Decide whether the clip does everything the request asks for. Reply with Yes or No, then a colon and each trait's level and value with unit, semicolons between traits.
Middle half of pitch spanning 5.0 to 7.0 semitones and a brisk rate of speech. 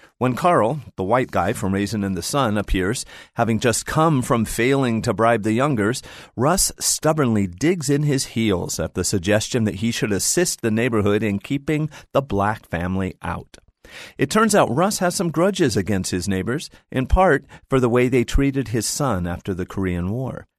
No: wide, 5.6 semitones; average, 185 wpm